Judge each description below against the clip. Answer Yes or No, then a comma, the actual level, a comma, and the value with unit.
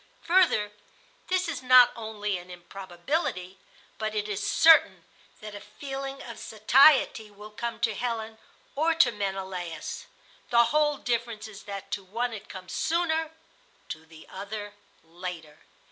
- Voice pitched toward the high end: Yes, high, 215 Hz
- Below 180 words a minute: Yes, average, 140 wpm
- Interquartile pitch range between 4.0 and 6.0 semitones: Yes, average, 4.7 semitones